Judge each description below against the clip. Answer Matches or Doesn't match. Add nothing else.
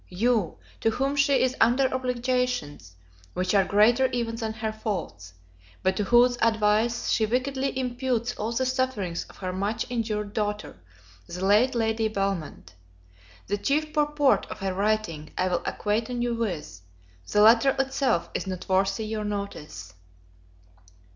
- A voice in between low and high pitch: Doesn't match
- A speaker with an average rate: Matches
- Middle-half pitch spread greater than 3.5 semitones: Matches